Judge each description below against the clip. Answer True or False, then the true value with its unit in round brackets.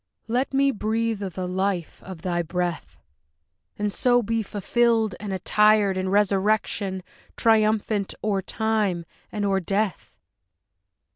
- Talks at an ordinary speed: False (125 wpm)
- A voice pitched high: True (205 Hz)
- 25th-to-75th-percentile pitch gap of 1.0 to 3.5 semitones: True (2.6 semitones)